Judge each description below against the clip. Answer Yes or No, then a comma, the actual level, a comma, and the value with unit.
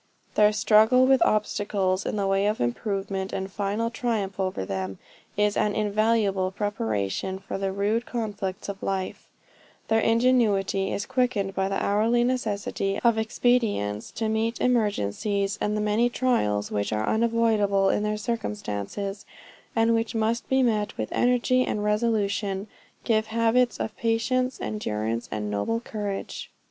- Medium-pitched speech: No, high, 210 Hz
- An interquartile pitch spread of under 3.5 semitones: Yes, average, 2.8 semitones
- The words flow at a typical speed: Yes, average, 145 wpm